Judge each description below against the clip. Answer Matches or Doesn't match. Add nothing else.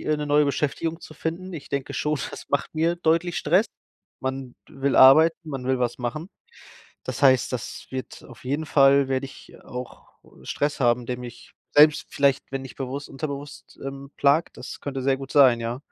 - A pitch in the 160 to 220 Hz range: Doesn't match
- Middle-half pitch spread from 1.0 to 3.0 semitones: Matches